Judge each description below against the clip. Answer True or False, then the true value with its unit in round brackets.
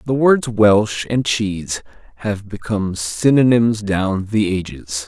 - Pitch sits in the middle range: False (105 Hz)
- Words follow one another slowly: True (130 wpm)